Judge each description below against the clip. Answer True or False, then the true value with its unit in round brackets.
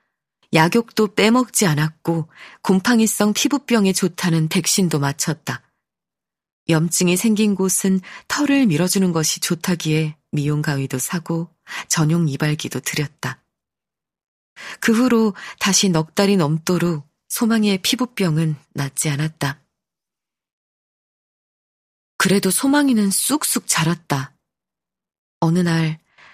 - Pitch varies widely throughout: False (4.8 semitones)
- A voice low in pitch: False (175 Hz)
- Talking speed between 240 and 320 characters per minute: False (230 characters per minute)